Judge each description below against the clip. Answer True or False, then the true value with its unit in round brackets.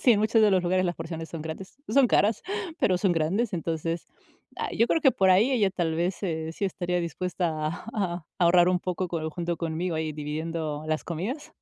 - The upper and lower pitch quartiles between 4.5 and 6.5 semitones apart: False (2.9 semitones)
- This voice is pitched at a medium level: True (175 Hz)